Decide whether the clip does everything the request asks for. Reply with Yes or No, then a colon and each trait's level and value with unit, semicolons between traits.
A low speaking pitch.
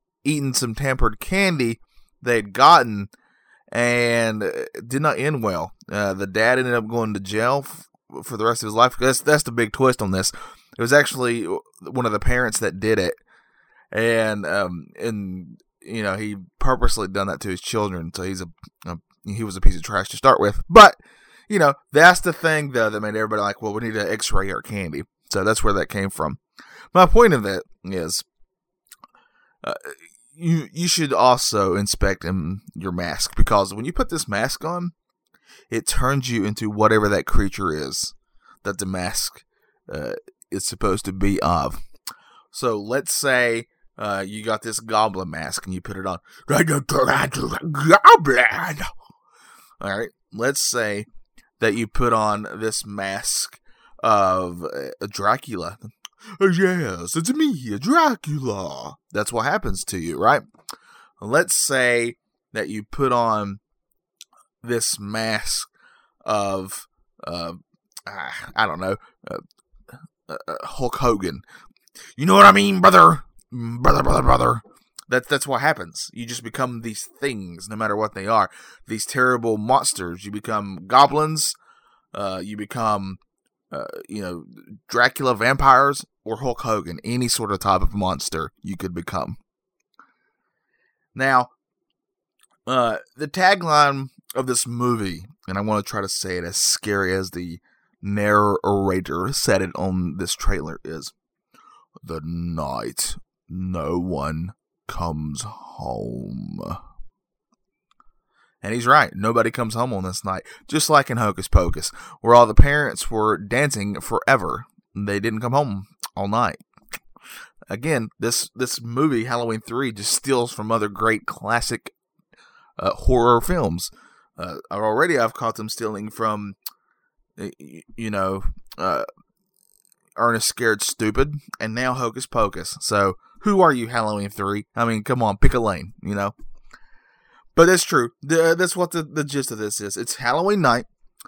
Yes: low, 110 Hz